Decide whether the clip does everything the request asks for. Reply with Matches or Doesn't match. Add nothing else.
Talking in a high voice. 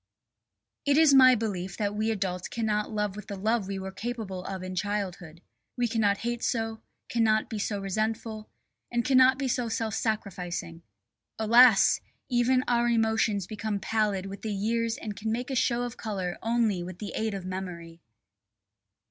Matches